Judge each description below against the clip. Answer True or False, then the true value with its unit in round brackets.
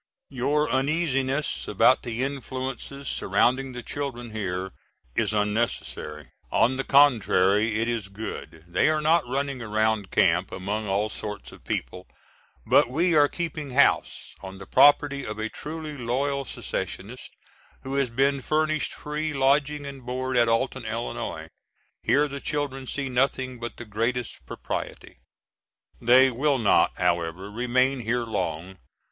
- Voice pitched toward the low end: True (125 Hz)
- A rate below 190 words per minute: True (140 wpm)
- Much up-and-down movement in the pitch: False (4.5 semitones)